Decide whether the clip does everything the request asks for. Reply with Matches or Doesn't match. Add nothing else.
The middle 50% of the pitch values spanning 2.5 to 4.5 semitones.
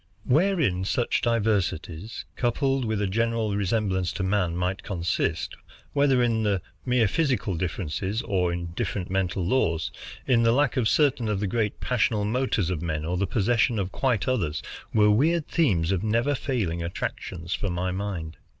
Doesn't match